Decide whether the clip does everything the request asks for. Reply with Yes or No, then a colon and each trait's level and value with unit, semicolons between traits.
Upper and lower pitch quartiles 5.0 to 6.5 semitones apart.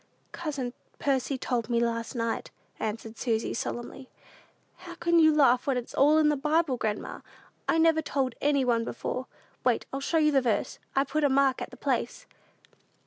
No: average, 4.1 semitones